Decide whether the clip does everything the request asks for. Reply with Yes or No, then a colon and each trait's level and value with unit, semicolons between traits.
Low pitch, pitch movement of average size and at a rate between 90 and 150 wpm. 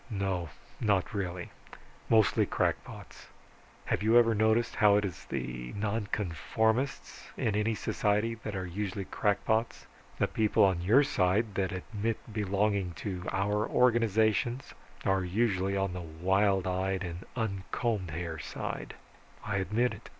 Yes: low, 100 Hz; average, 3.0 semitones; slow, 135 wpm